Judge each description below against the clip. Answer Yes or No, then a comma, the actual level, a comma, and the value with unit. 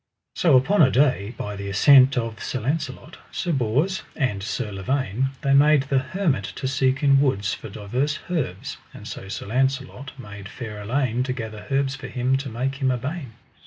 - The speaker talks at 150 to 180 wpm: No, average, 190 wpm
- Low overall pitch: Yes, low, 130 Hz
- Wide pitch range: No, average, 3.7 semitones